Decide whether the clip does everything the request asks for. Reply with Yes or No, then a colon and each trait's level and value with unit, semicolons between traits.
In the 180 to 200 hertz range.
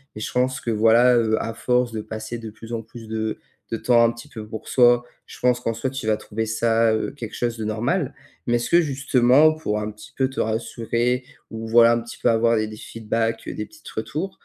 No: low, 115 Hz